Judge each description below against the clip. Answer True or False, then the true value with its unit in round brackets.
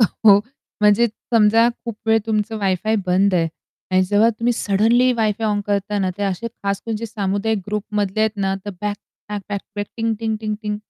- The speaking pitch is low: False (210 Hz)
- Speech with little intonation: True (1.9 semitones)